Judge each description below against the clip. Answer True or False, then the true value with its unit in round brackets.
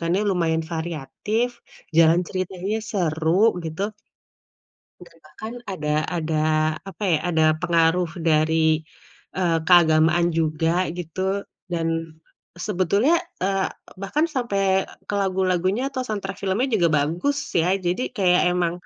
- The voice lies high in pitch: False (180 Hz)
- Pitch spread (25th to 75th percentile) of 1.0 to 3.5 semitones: True (3.1 semitones)